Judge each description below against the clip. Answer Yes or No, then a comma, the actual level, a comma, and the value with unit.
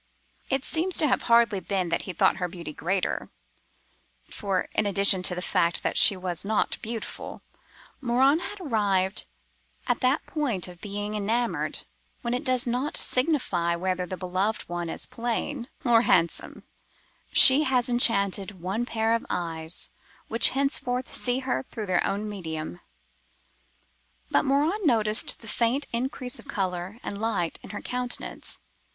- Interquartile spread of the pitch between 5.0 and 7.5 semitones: Yes, average, 5.3 semitones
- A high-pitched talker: Yes, high, 215 Hz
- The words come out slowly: No, average, 150 wpm